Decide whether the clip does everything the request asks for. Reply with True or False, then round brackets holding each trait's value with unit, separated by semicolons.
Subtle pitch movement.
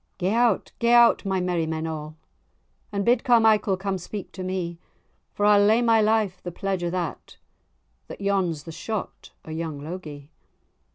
False (4.1 semitones)